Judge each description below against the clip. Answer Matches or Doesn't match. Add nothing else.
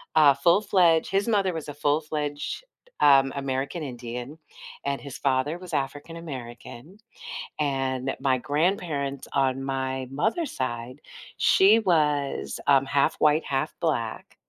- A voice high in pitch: Doesn't match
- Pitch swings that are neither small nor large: Matches